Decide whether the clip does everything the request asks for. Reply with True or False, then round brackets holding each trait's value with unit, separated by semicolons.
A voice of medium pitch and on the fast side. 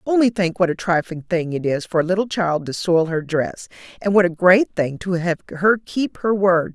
True (180 Hz; 240 wpm)